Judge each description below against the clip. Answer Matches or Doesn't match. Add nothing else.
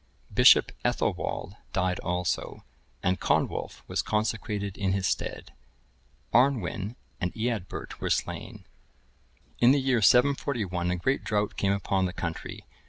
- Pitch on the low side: Matches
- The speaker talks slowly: Matches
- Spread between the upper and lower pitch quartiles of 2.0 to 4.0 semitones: Doesn't match